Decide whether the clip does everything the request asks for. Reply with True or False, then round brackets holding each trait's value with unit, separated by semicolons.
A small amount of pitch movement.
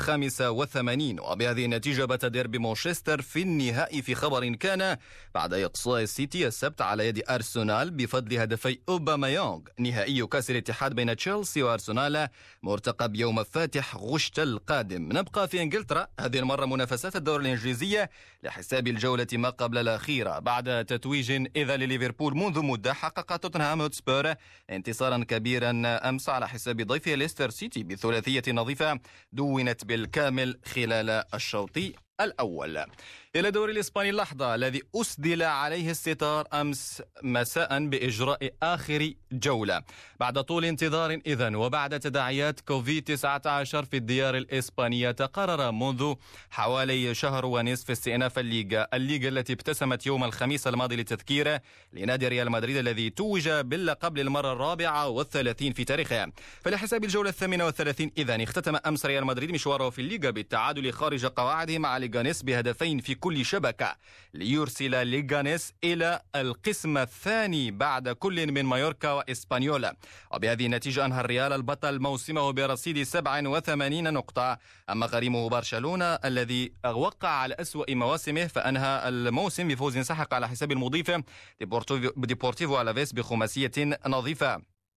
False (3.7 semitones)